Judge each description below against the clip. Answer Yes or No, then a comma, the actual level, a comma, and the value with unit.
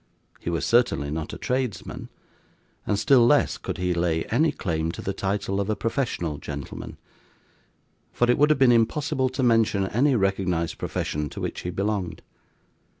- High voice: No, low, 100 Hz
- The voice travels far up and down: Yes, wide, 6.2 semitones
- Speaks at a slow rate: No, average, 165 wpm